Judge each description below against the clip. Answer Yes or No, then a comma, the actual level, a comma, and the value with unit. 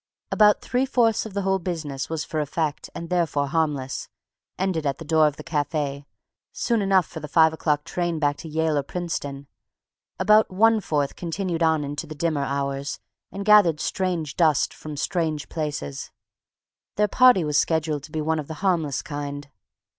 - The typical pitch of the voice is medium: Yes, medium, 160 Hz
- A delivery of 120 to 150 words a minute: No, average, 175 wpm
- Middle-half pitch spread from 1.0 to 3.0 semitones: No, average, 3.6 semitones